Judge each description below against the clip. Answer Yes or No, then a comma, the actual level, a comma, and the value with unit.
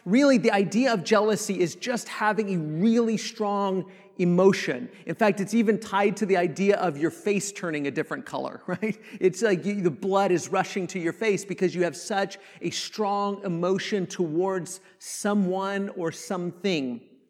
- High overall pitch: Yes, high, 195 Hz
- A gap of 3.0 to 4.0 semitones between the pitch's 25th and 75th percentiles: No, narrow, 2.4 semitones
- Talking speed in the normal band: Yes, average, 170 wpm